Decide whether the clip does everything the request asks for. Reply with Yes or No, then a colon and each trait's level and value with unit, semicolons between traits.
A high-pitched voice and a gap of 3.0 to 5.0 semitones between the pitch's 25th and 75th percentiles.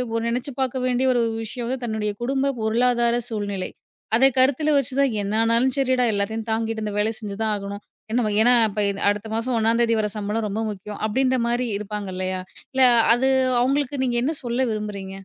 Yes: high, 225 Hz; average, 3.3 semitones